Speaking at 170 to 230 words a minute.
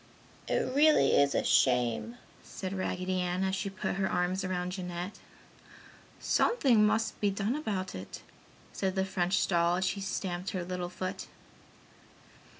No: average, 150 wpm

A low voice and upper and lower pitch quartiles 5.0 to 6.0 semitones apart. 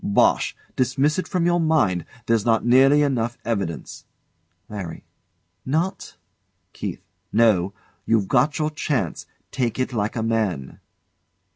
Yes: low, 120 Hz; average, 5.3 semitones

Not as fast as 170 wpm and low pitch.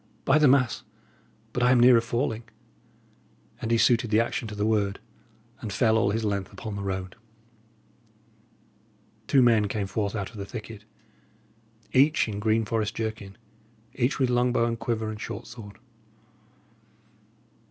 Yes: average, 155 wpm; low, 110 Hz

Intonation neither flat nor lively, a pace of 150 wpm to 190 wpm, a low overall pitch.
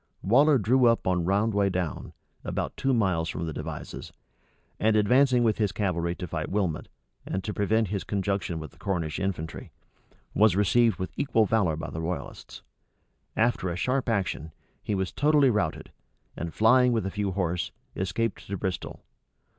Yes: average, 4.1 semitones; average, 160 wpm; low, 100 Hz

